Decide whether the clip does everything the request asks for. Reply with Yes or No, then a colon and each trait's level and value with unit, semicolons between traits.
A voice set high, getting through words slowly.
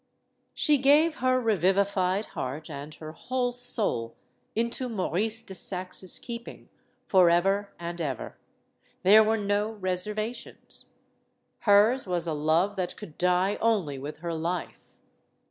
Yes: high, 195 Hz; slow, 125 wpm